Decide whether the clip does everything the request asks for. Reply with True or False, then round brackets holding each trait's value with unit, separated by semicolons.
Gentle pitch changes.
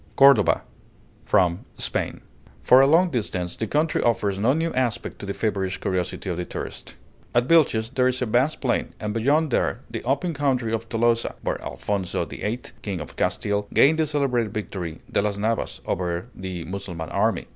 False (5.1 semitones)